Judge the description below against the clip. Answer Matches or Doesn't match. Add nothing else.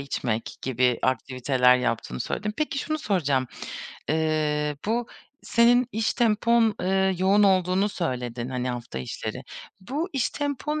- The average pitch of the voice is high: Doesn't match